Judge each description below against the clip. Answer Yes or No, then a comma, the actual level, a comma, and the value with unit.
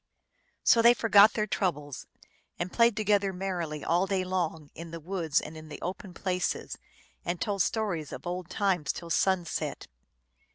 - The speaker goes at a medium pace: Yes, average, 165 wpm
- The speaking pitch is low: No, medium, 180 Hz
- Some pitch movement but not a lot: Yes, average, 3.1 semitones